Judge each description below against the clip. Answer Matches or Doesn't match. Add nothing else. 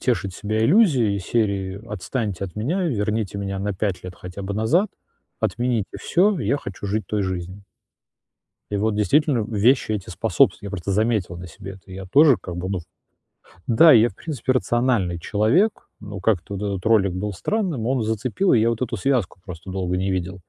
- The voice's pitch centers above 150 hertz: Doesn't match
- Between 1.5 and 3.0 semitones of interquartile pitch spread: Doesn't match